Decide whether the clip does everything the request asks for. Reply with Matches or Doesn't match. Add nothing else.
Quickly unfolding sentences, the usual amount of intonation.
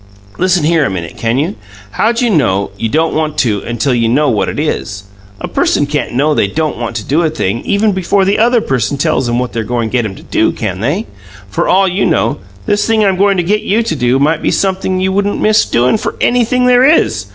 Doesn't match